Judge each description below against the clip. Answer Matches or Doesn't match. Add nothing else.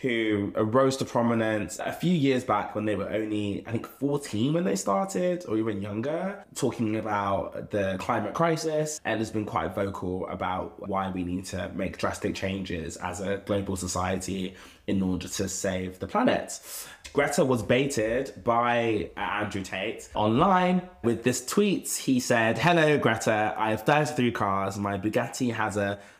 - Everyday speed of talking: Matches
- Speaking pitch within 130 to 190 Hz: Doesn't match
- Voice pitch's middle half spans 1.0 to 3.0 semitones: Doesn't match